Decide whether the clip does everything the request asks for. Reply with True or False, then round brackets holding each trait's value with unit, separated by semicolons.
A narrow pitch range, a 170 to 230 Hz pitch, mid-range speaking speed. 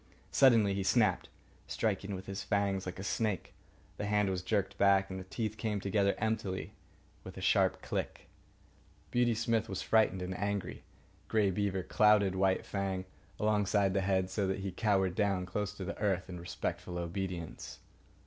False (1.8 semitones; 100 Hz; 170 wpm)